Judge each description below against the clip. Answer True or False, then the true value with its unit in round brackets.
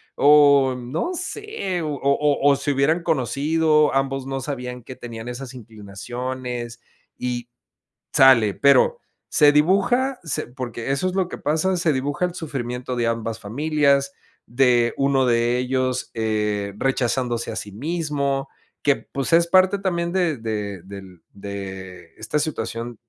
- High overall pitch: False (135 Hz)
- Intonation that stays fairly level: False (4.3 semitones)